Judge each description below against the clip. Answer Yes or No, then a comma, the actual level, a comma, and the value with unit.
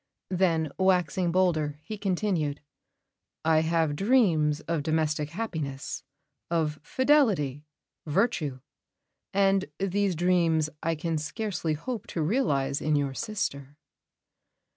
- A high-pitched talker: No, medium, 165 Hz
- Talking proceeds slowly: Yes, slow, 105 wpm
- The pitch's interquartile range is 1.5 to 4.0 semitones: No, average, 4.4 semitones